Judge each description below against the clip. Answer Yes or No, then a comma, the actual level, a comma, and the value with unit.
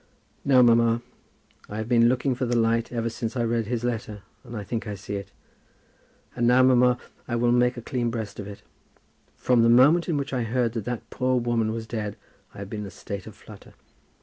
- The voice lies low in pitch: Yes, low, 115 Hz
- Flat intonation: Yes, narrow, 1.9 semitones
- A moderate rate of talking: No, fast, 230 wpm